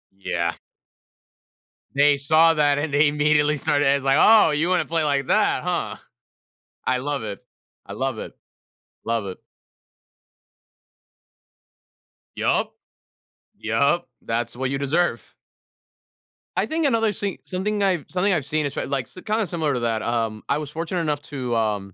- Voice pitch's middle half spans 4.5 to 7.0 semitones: Yes, average, 4.8 semitones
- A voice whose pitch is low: No, medium, 145 Hz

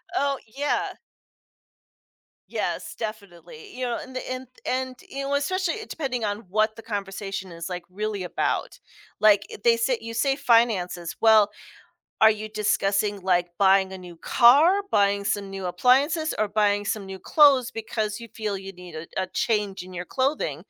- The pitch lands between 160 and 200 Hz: No, high, 215 Hz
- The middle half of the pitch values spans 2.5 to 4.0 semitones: No, average, 4.7 semitones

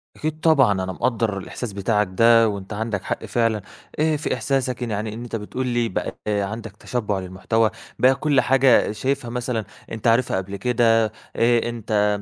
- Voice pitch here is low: Yes, low, 115 Hz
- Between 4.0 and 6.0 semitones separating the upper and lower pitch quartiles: No, average, 3.1 semitones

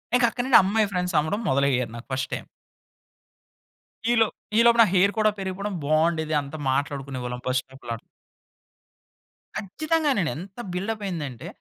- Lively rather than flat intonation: Yes, wide, 7.5 semitones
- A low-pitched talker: No, medium, 180 Hz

